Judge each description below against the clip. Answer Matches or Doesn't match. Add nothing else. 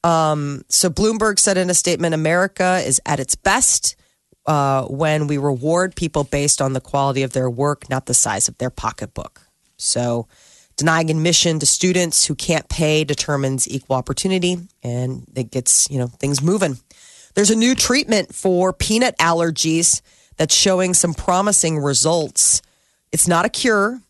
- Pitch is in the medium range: Matches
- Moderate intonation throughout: Matches